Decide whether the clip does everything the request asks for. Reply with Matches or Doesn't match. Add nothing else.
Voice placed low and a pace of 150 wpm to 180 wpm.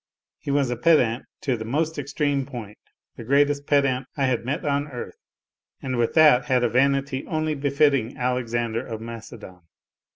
Matches